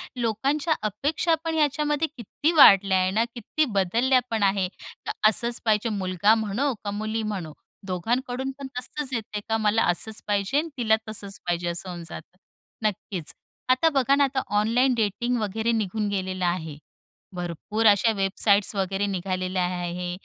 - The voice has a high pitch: Yes, high, 215 Hz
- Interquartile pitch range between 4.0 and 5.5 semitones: Yes, average, 4.8 semitones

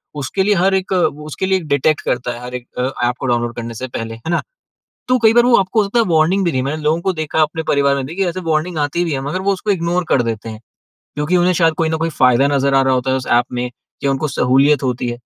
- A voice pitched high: No, medium, 150 Hz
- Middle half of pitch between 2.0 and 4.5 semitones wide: No, wide, 5.6 semitones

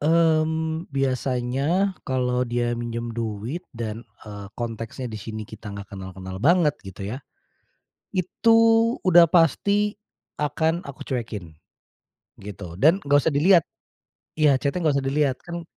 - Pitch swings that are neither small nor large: No, wide, 6.4 semitones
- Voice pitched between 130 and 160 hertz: Yes, low, 135 Hz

